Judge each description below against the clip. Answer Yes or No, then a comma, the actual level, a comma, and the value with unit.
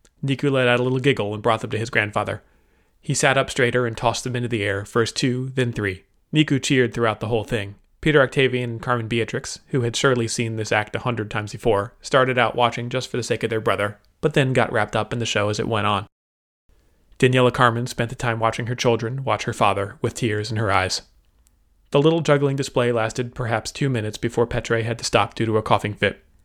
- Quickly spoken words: Yes, fast, 235 wpm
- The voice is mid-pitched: No, low, 115 Hz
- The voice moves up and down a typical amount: Yes, average, 3.0 semitones